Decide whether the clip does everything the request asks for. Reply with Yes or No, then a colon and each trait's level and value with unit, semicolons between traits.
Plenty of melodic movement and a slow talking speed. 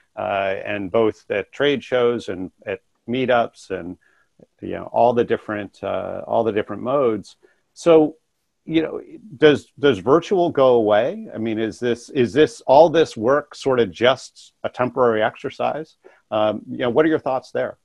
No: wide, 5.9 semitones; average, 170 wpm